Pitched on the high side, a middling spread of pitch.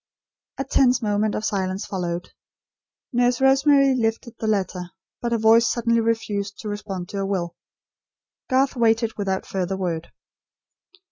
Yes: high, 215 Hz; average, 3.7 semitones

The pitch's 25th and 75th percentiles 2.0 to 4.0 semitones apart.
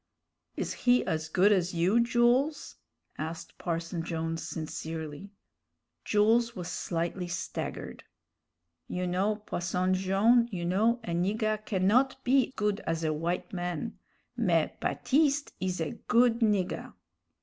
No: average, 5.3 semitones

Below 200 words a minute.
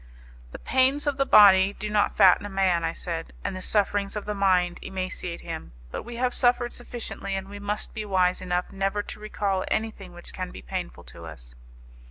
No: fast, 205 wpm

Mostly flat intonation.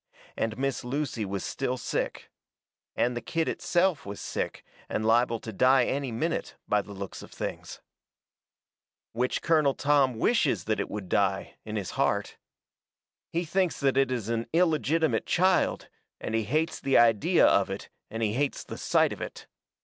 No: wide, 5.4 semitones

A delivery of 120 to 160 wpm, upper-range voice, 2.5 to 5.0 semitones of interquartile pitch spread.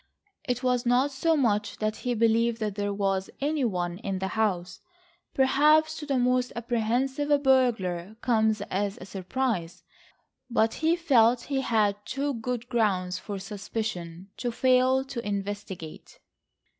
Yes: average, 140 wpm; high, 230 Hz; average, 4.6 semitones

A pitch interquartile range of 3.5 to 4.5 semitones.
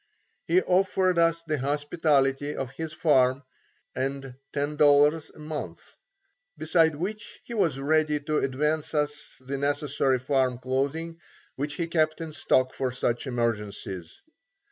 No: average, 2.9 semitones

